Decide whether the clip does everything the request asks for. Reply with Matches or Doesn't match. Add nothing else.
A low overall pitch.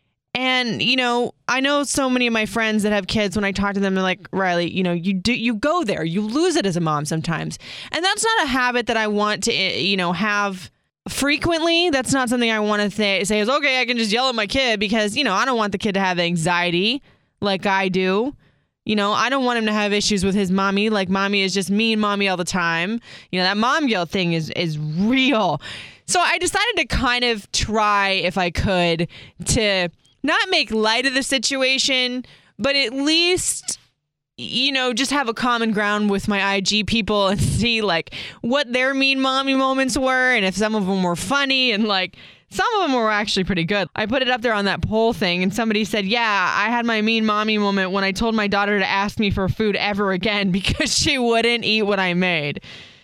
Doesn't match